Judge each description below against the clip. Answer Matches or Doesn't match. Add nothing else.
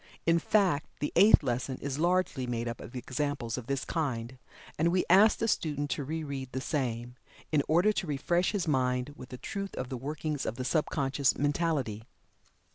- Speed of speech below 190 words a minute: Doesn't match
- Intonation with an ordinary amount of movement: Matches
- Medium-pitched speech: Matches